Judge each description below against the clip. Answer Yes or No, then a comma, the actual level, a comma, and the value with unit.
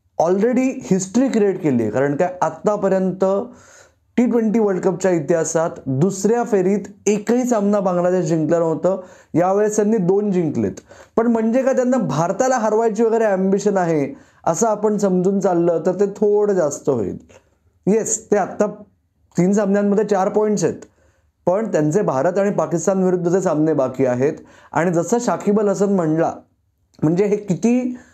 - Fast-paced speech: Yes, fast, 145 wpm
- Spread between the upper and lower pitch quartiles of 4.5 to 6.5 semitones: No, average, 3.8 semitones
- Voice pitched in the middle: No, high, 195 Hz